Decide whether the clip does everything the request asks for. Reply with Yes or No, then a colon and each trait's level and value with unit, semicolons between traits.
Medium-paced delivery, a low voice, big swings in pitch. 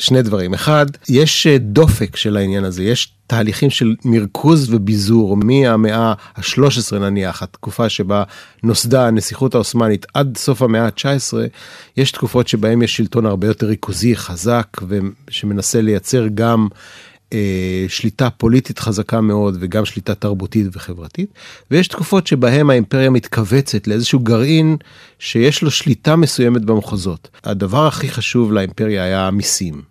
No: average, 130 wpm; low, 115 Hz; average, 4.1 semitones